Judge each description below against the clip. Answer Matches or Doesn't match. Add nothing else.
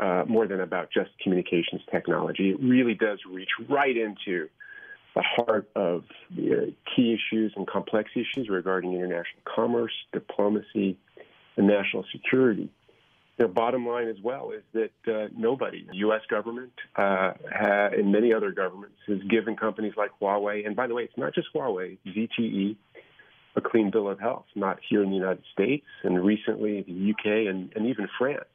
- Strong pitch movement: Doesn't match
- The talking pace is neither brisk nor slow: Matches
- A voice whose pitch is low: Matches